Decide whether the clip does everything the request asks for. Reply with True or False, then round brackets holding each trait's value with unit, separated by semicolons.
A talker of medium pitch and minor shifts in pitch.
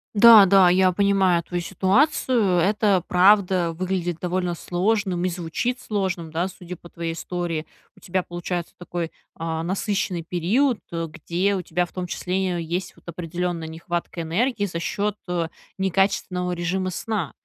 True (180 Hz; 2.2 semitones)